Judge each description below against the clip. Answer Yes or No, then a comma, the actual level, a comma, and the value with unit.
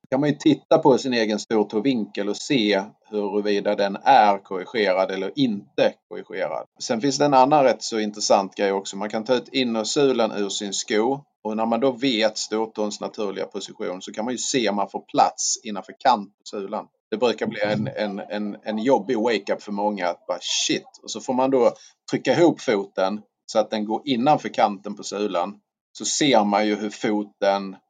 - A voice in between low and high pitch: No, low, 105 Hz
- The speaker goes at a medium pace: No, fast, 200 wpm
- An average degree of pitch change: No, narrow, 1.8 semitones